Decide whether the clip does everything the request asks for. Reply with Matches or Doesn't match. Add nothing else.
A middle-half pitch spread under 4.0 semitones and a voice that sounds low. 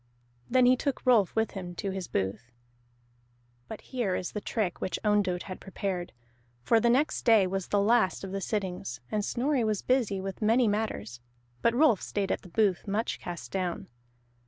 Doesn't match